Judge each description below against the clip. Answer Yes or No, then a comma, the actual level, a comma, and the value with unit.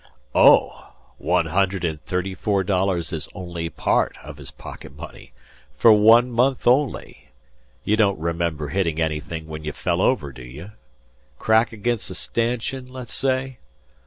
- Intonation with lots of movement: Yes, wide, 6.4 semitones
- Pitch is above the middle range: No, very low, 95 Hz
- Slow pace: No, average, 150 wpm